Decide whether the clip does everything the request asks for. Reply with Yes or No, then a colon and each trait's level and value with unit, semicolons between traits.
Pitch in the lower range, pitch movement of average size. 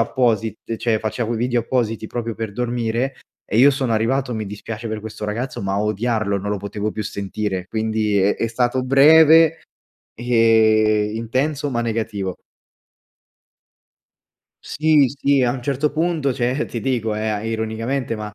Yes: low, 115 Hz; average, 3.1 semitones